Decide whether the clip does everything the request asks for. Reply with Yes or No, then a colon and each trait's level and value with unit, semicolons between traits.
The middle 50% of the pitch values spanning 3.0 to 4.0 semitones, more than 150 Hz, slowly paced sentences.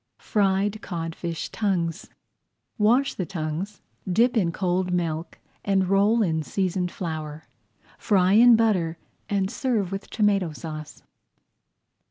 Yes: average, 3.7 semitones; high, 190 Hz; slow, 115 wpm